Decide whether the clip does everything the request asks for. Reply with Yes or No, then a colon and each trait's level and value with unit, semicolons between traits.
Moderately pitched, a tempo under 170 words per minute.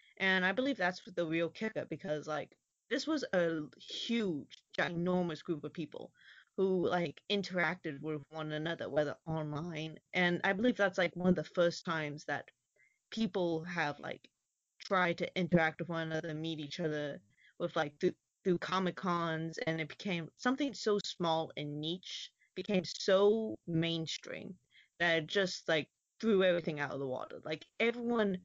Yes: medium, 170 Hz; average, 160 wpm